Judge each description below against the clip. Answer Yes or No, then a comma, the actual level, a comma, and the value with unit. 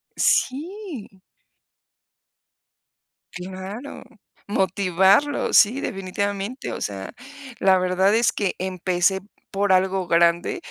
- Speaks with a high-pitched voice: Yes, high, 195 Hz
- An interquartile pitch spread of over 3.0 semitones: No, narrow, 2.5 semitones